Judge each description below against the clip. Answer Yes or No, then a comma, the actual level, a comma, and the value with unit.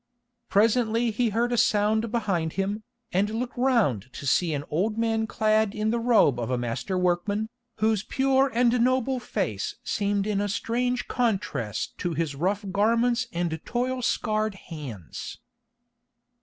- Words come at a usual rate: Yes, average, 150 wpm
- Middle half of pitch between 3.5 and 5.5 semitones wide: Yes, average, 5.0 semitones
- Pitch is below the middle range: No, high, 215 Hz